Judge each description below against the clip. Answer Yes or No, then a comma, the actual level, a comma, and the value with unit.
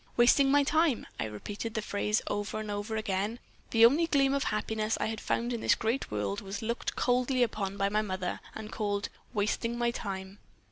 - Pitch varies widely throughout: No, average, 2.9 semitones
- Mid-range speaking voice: No, high, 220 Hz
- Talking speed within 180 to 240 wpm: Yes, average, 195 wpm